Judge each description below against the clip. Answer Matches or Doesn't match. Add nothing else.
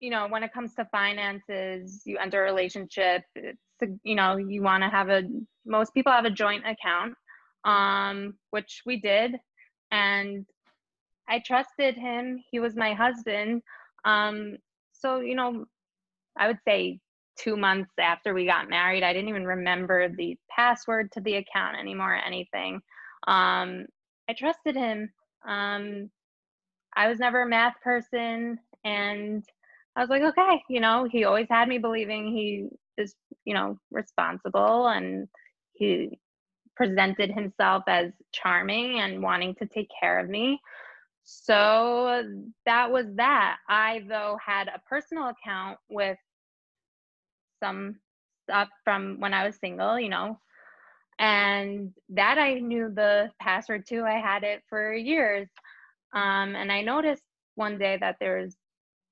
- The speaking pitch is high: Matches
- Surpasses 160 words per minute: Doesn't match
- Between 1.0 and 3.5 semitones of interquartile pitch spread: Matches